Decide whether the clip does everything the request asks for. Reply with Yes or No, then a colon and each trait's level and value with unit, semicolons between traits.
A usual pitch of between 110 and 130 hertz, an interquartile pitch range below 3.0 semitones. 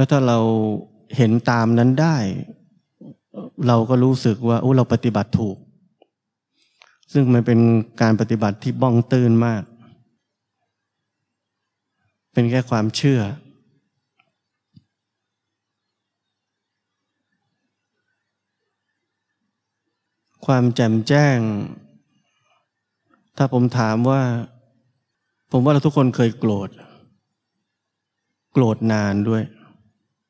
Yes: low, 115 Hz; narrow, 2.4 semitones